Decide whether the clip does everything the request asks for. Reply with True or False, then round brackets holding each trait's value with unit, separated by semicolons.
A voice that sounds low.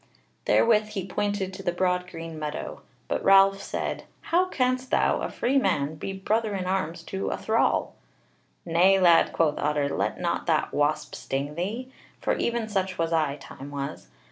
False (185 Hz)